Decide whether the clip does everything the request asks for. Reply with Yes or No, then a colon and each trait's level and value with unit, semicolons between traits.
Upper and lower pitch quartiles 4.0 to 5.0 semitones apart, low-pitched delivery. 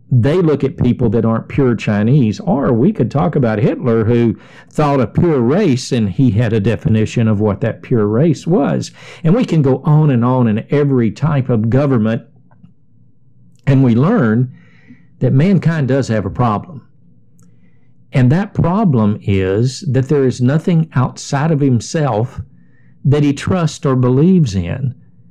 Yes: average, 4.3 semitones; low, 130 Hz